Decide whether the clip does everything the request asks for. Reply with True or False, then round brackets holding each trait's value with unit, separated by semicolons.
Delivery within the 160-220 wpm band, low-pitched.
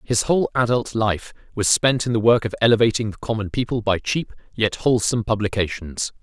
True (185 wpm; 110 Hz)